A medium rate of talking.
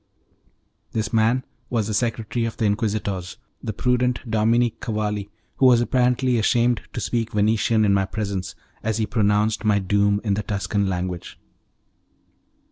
Yes: average, 145 wpm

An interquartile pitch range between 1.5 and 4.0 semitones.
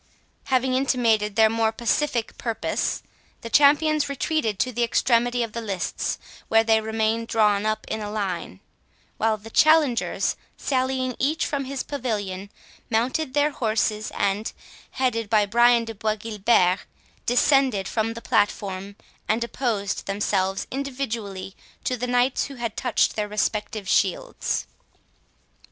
Yes: average, 3.5 semitones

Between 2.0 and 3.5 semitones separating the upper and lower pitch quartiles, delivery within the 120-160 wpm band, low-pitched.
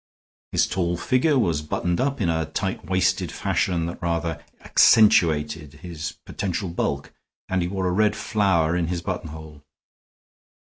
Yes: average, 3.0 semitones; average, 145 wpm; very low, 85 Hz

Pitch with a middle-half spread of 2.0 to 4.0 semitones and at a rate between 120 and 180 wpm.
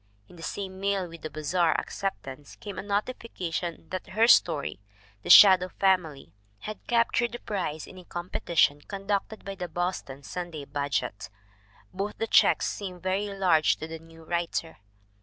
Yes: average, 3.7 semitones; average, 160 wpm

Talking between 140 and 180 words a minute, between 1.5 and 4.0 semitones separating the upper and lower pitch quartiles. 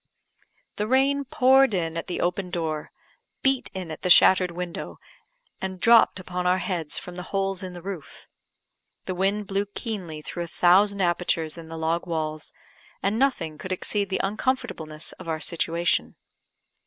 Yes: average, 165 wpm; average, 3.2 semitones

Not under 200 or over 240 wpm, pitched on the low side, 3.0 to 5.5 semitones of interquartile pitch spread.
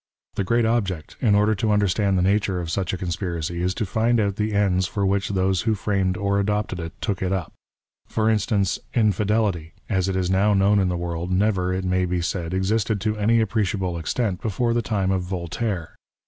No: fast, 205 wpm; very low, 95 Hz; narrow, 2.5 semitones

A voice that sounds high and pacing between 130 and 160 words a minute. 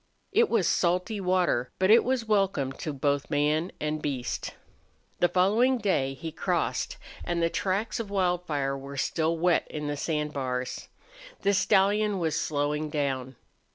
No: medium, 165 Hz; average, 155 wpm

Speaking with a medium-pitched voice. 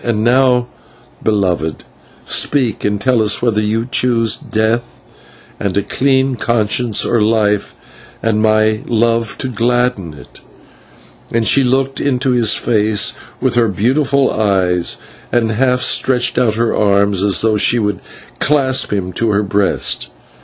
No: low, 115 Hz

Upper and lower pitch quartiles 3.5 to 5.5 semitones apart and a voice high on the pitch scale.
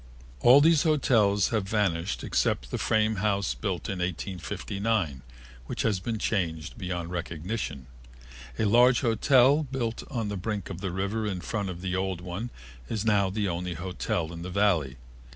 No: average, 3.9 semitones; low, 100 Hz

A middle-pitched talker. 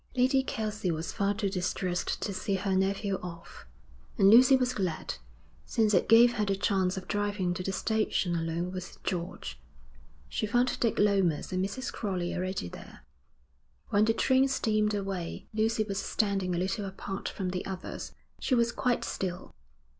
No: high, 195 Hz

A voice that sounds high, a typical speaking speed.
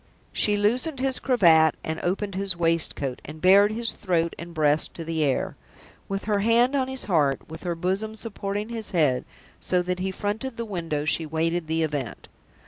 No: medium, 180 Hz; average, 185 wpm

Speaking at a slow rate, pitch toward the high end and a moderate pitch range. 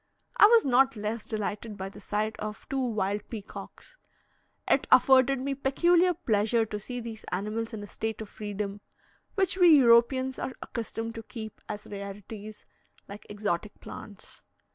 No: average, 155 wpm; high, 220 Hz; average, 3.8 semitones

